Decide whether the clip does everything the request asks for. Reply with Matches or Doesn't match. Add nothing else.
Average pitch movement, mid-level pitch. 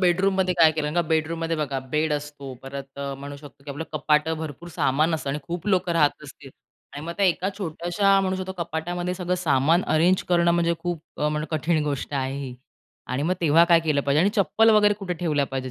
Matches